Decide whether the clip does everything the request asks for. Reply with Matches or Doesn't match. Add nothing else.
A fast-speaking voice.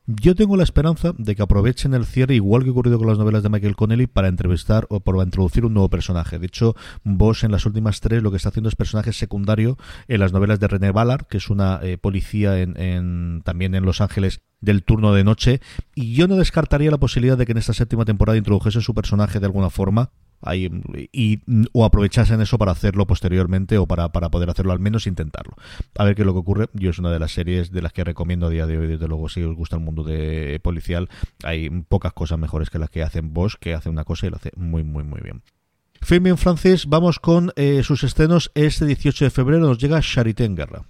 Matches